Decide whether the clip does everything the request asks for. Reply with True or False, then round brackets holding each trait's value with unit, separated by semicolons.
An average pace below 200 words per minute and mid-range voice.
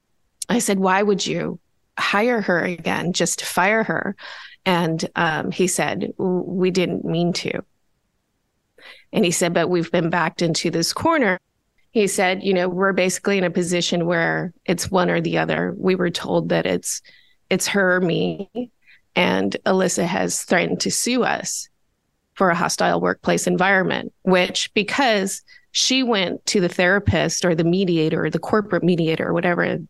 True (165 wpm; 180 Hz)